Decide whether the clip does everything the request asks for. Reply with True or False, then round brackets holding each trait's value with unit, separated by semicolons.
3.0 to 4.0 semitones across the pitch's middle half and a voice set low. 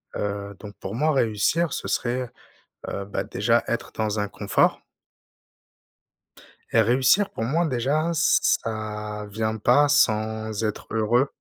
True (3.6 semitones; 110 Hz)